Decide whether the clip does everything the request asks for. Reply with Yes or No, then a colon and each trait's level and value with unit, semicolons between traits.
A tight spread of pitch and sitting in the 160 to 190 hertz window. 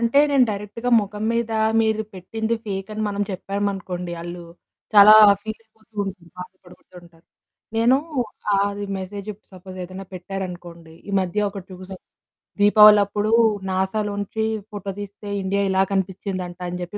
No: narrow, 2.2 semitones; high, 200 Hz